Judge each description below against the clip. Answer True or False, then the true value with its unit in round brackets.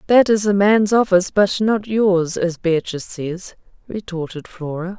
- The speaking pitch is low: False (190 Hz)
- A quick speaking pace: False (155 wpm)